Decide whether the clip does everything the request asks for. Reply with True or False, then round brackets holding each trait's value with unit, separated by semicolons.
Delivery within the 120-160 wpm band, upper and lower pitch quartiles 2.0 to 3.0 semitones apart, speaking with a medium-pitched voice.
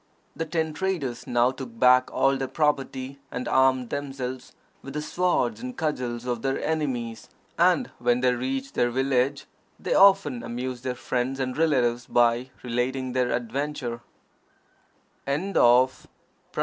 False (135 wpm; 2.4 semitones; 130 Hz)